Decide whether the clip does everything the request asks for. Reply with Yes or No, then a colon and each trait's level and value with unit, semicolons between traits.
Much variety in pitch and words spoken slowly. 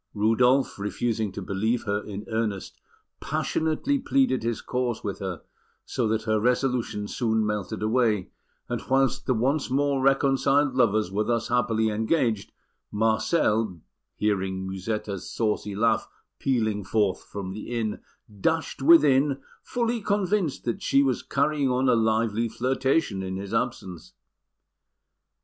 No: average, 4.2 semitones; slow, 130 wpm